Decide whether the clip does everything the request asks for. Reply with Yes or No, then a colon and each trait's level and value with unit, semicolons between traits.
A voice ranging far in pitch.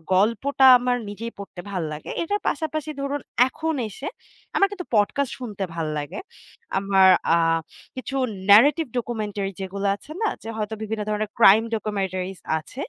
Yes: wide, 5.9 semitones